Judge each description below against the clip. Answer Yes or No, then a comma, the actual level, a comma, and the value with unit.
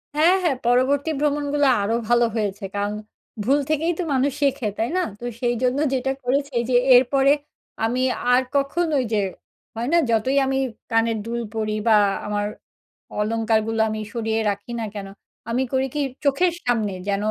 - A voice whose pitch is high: Yes, high, 245 Hz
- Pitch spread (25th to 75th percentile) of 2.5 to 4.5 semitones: Yes, average, 4.0 semitones